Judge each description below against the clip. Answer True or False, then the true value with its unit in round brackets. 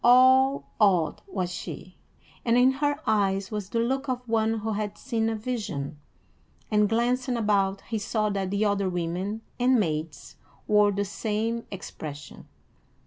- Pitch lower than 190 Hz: False (215 Hz)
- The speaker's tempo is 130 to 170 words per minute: True (150 wpm)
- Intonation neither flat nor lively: True (3.5 semitones)